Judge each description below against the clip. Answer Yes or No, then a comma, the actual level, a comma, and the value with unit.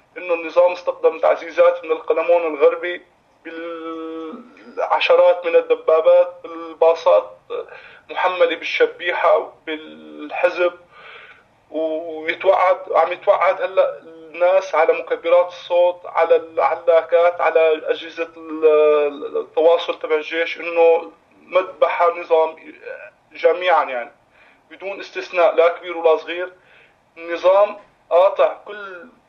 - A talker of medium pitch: Yes, medium, 175 Hz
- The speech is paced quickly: No, average, 90 wpm